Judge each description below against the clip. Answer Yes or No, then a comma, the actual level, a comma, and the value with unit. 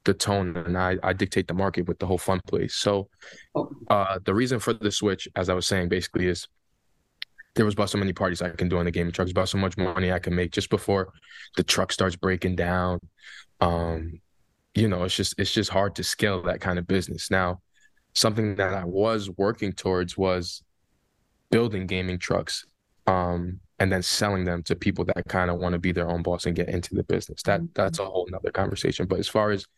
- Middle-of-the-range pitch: No, very low, 95 Hz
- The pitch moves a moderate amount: No, narrow, 1.9 semitones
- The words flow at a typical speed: No, fast, 220 wpm